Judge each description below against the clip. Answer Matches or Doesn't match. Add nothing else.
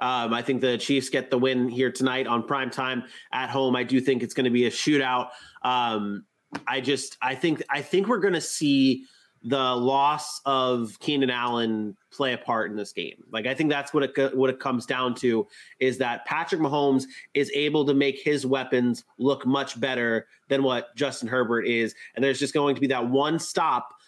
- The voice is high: Doesn't match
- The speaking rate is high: Matches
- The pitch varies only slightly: Matches